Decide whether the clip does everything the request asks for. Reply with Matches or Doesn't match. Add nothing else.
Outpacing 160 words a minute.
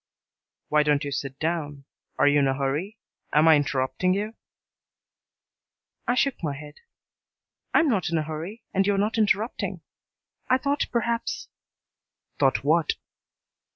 Doesn't match